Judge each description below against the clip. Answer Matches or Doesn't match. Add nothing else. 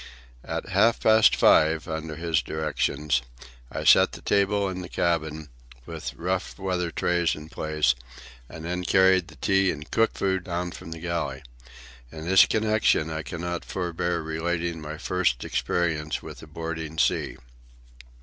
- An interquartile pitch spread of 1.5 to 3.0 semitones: Matches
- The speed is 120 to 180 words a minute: Matches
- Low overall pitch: Matches